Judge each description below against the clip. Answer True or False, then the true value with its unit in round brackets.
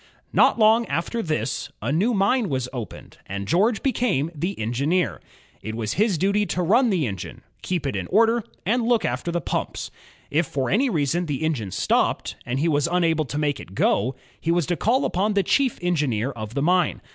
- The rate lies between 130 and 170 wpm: False (200 wpm)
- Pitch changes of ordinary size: False (7.1 semitones)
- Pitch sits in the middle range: True (170 Hz)